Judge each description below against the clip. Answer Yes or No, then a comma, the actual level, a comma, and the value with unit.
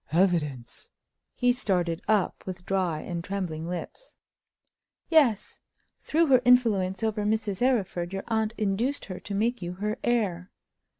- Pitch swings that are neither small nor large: Yes, average, 4.6 semitones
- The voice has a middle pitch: No, high, 200 Hz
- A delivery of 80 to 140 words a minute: Yes, slow, 135 wpm